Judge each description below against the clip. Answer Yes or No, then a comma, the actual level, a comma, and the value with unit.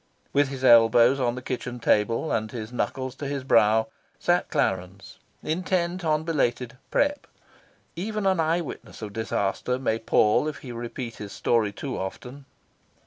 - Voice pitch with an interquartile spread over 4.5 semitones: Yes, average, 5.2 semitones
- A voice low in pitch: Yes, low, 125 Hz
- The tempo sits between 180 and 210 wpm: No, average, 155 wpm